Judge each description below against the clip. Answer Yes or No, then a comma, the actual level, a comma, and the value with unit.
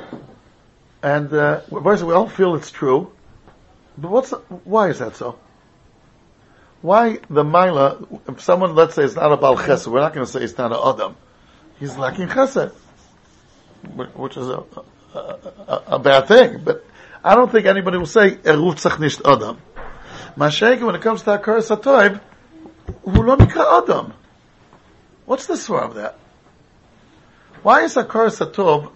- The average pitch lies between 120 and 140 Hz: No, high, 195 Hz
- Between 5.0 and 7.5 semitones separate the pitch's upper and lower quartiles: Yes, wide, 5.5 semitones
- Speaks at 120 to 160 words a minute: Yes, average, 145 wpm